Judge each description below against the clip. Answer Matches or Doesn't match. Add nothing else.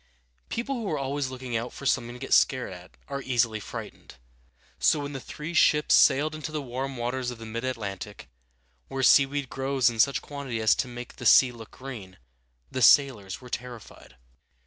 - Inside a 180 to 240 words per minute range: Matches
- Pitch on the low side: Matches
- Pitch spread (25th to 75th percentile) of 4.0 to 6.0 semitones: Doesn't match